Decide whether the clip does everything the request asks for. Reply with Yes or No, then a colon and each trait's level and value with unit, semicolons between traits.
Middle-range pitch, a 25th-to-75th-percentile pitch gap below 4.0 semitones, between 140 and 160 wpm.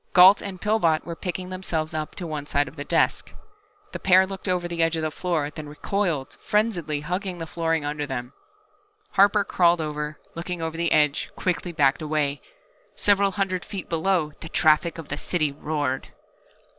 No: medium, 165 Hz; average, 3.5 semitones; average, 180 wpm